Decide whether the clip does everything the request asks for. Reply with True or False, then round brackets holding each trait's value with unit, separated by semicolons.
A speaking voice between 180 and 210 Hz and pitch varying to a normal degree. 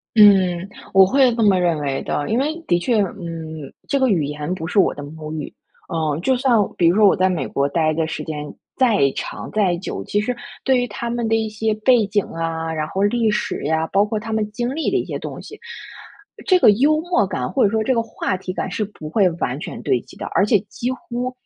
False (200 Hz; 6.1 semitones)